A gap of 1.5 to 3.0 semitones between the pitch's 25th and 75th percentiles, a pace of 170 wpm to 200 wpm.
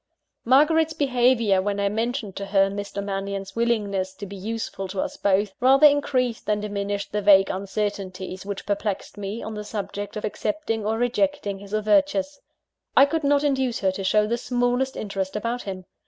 No: average, 3.8 semitones; average, 175 wpm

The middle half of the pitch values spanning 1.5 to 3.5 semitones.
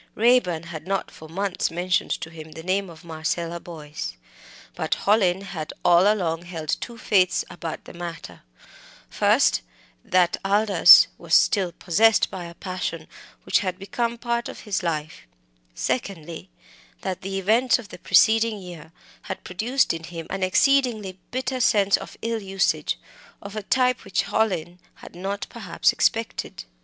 No: average, 4.0 semitones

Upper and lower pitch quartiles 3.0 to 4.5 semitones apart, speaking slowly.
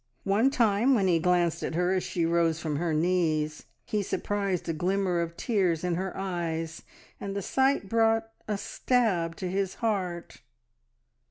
No: average, 3.3 semitones; average, 165 wpm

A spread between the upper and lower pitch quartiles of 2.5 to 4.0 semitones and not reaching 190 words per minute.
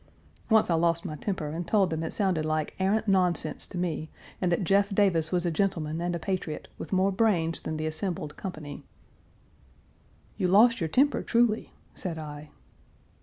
Yes: average, 3.7 semitones; average, 175 wpm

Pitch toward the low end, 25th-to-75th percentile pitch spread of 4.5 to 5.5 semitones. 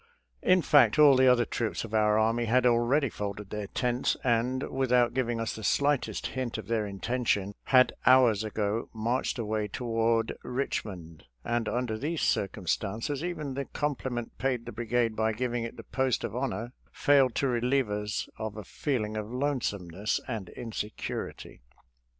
No: low, 120 Hz; average, 3.1 semitones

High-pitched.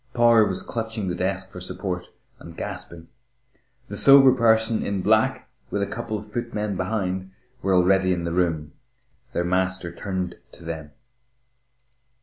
No: very low, 95 Hz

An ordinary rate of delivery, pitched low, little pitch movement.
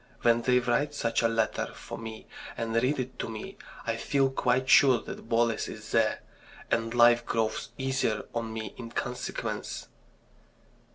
Yes: average, 160 wpm; low, 115 Hz; narrow, 1.9 semitones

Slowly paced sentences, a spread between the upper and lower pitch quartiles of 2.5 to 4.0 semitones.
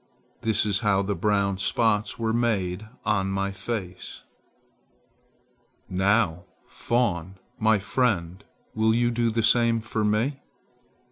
Yes: slow, 120 wpm; average, 2.9 semitones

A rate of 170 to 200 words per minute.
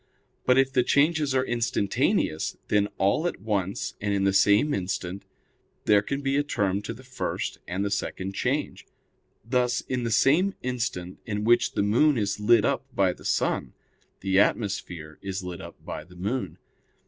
Yes: average, 175 wpm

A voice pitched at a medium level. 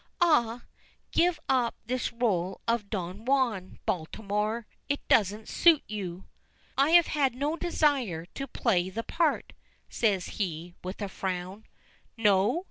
No: high, 220 Hz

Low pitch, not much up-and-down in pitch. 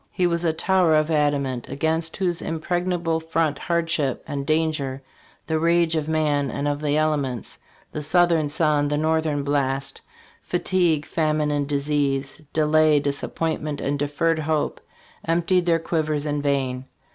No: medium, 155 Hz; narrow, 2.3 semitones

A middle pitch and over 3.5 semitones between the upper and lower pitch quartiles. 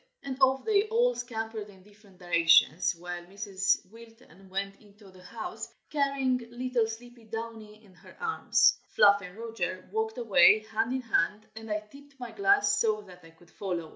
No: high, 220 Hz; average, 4.3 semitones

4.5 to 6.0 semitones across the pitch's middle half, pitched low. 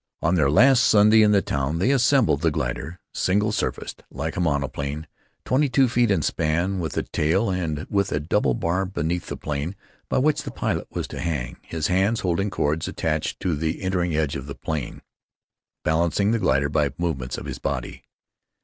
Yes: average, 5.0 semitones; very low, 85 Hz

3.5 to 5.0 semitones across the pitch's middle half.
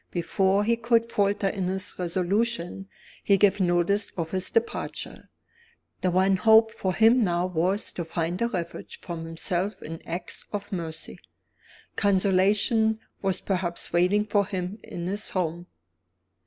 No: average, 2.9 semitones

